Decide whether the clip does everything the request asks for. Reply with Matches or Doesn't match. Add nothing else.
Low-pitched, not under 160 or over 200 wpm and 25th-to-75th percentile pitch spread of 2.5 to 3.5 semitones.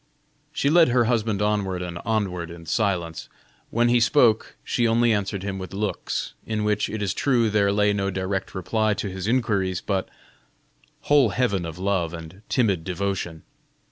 Matches